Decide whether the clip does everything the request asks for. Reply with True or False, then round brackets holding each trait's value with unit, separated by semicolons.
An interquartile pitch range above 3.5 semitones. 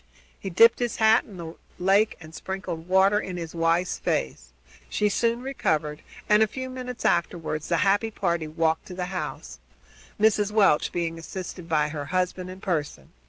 True (4.2 semitones)